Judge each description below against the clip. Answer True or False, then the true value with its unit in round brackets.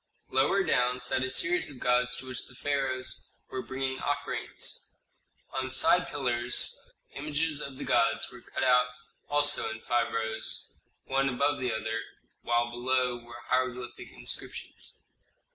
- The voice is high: False (130 Hz)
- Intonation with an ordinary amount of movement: False (2.2 semitones)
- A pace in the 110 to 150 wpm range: True (145 wpm)